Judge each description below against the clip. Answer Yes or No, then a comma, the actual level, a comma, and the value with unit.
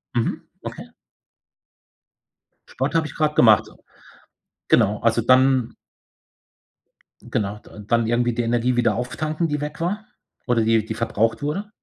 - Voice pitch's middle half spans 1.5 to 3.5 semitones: No, average, 4.6 semitones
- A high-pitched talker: No, low, 120 Hz